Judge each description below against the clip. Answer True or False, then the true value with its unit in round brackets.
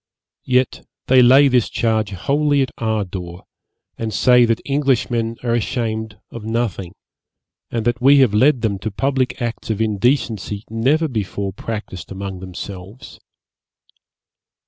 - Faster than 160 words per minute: False (135 wpm)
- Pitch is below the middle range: True (115 Hz)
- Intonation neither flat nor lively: True (3.7 semitones)